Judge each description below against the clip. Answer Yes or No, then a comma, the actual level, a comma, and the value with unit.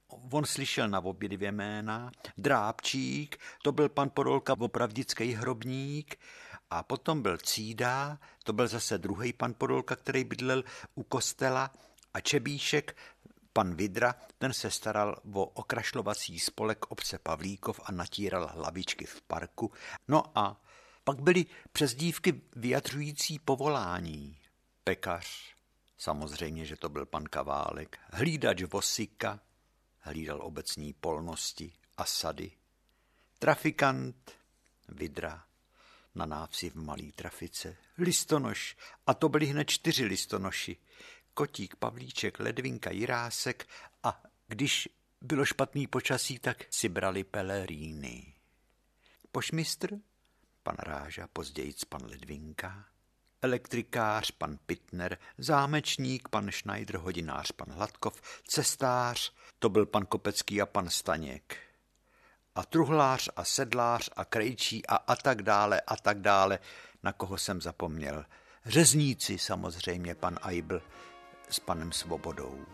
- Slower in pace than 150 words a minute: Yes, slow, 115 wpm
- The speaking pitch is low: Yes, low, 110 Hz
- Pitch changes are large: Yes, wide, 7.3 semitones